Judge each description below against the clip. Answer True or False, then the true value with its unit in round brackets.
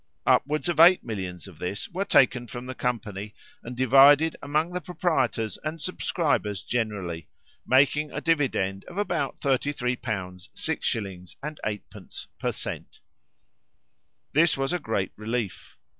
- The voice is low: True (125 Hz)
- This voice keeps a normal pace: False (130 wpm)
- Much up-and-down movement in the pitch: True (6.7 semitones)